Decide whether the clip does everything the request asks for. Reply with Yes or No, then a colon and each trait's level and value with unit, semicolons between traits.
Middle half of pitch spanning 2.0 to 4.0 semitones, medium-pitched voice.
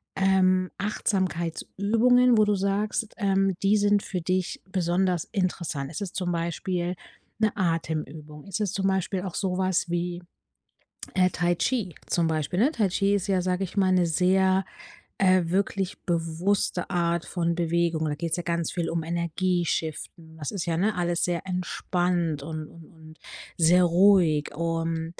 Yes: narrow, 2.4 semitones; medium, 180 Hz